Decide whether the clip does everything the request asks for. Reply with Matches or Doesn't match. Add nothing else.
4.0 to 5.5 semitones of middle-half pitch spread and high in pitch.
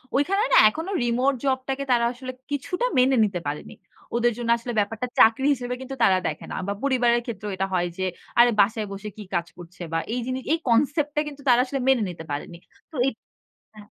Matches